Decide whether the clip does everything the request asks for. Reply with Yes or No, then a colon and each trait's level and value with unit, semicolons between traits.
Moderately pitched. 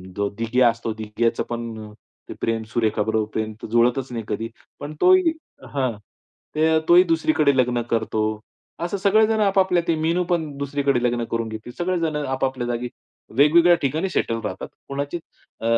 No: low, 130 Hz